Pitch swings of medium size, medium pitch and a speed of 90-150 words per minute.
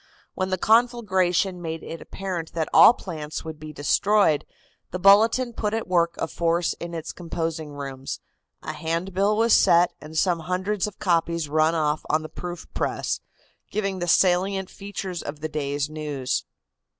No: average, 3.6 semitones; medium, 170 Hz; average, 165 wpm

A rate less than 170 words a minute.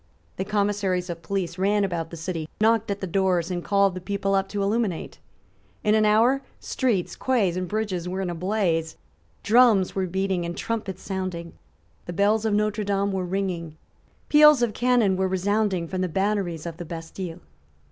No: average, 180 wpm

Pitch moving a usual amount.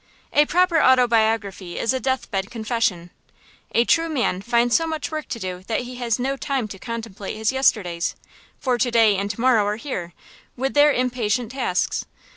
Yes: average, 4.0 semitones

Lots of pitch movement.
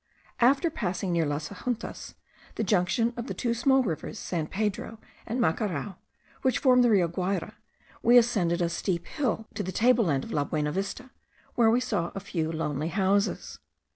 Yes: wide, 5.8 semitones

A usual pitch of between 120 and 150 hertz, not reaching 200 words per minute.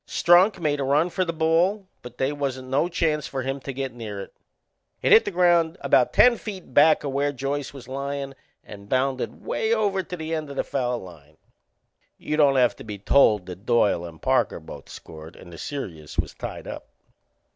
No: medium, 140 Hz; fast, 205 wpm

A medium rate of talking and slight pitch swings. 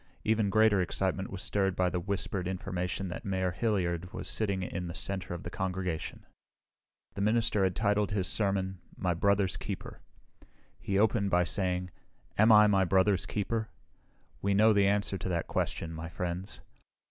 Yes: average, 165 wpm; narrow, 2.1 semitones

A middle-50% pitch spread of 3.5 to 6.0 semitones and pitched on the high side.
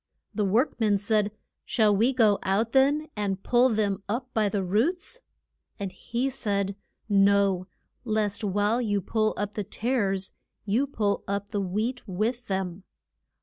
No: average, 2.9 semitones; high, 210 Hz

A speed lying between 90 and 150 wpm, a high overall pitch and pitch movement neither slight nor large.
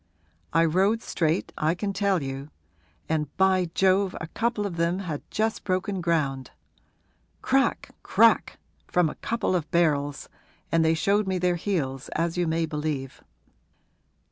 No: average, 145 wpm; medium, 170 Hz; average, 3.7 semitones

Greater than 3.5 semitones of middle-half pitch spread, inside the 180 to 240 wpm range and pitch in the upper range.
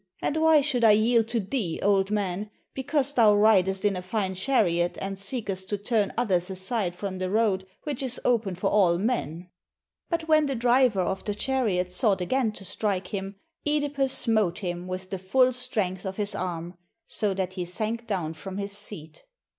Yes: average, 4.2 semitones; average, 190 wpm; high, 205 Hz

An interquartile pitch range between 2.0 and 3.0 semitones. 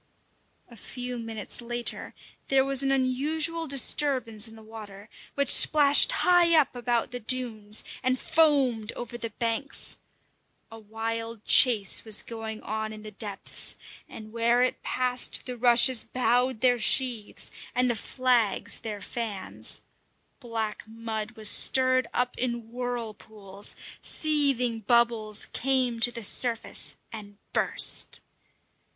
Yes: narrow, 2.6 semitones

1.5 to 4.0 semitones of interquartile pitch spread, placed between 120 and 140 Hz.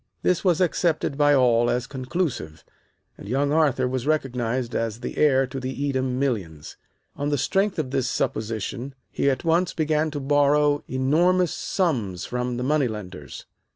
Yes: average, 3.6 semitones; low, 135 Hz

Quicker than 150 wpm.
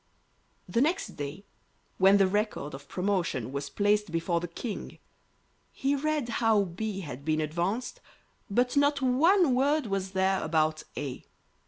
No: average, 145 wpm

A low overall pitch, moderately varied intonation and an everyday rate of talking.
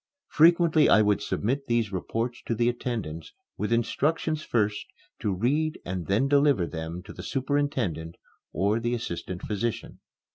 No: low, 115 Hz; wide, 6.1 semitones; average, 145 wpm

